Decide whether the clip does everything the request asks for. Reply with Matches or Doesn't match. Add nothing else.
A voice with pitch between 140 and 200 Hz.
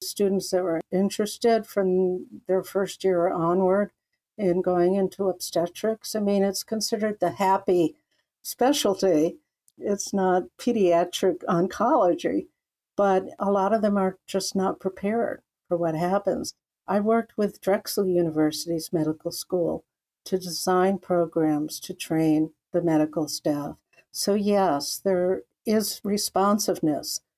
Matches